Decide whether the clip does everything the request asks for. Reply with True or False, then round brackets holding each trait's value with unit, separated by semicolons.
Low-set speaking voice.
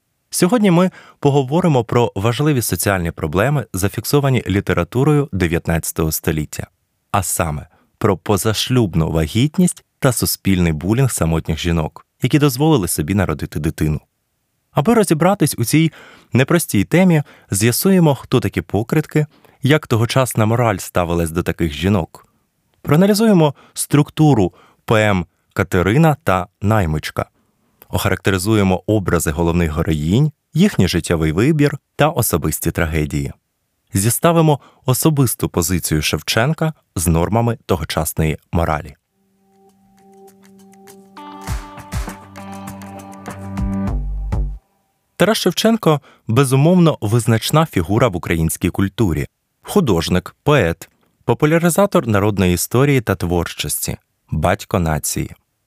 True (110 Hz)